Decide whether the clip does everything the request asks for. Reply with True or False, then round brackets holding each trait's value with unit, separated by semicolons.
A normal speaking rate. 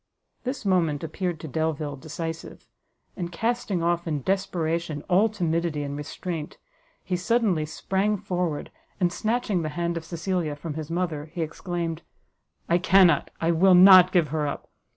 True (150 wpm)